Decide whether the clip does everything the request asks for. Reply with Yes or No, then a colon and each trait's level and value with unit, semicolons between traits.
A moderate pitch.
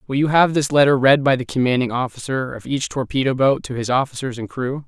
No: low, 130 Hz